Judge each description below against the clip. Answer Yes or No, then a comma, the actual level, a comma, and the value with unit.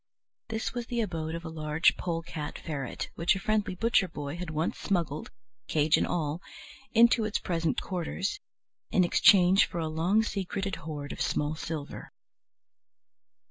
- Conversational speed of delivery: Yes, average, 150 wpm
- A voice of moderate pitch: Yes, medium, 170 Hz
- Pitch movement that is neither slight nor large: Yes, average, 3.9 semitones